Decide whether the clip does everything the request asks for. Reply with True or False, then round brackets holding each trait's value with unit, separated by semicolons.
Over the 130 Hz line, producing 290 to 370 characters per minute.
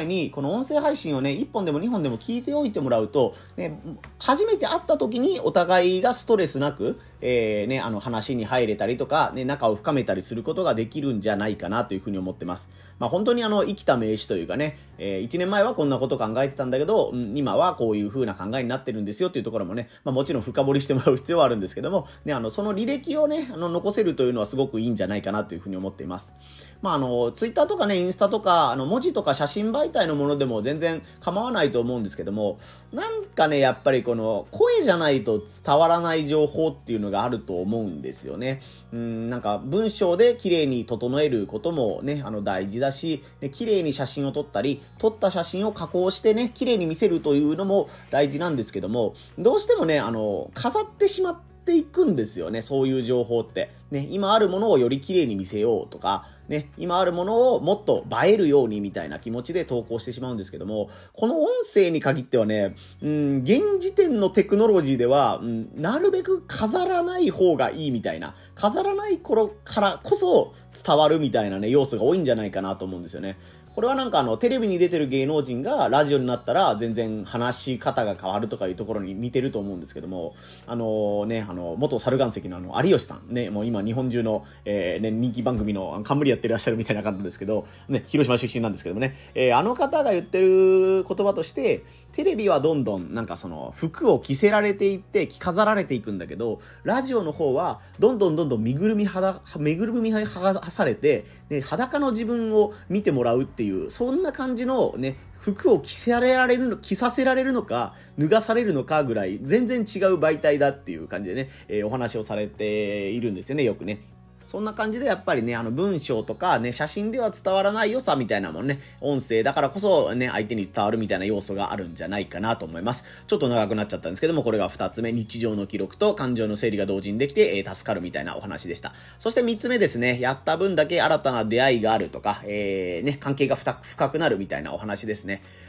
False (140 Hz; 430 characters per minute)